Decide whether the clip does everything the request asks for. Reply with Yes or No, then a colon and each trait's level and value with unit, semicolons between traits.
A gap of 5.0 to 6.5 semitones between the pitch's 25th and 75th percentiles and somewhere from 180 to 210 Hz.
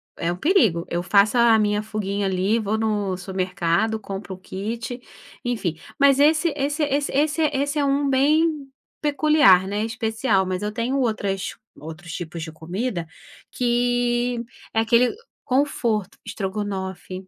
No: wide, 5.6 semitones; high, 220 Hz